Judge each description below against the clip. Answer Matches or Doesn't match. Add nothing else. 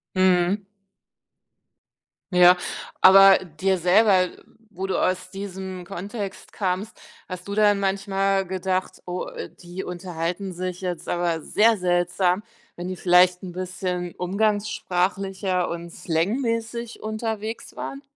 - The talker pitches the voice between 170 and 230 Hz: Matches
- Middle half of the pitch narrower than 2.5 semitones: Matches